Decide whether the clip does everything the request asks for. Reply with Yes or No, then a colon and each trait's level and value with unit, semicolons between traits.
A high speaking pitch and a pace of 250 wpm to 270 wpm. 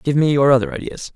No: medium, 140 Hz; fast, 260 wpm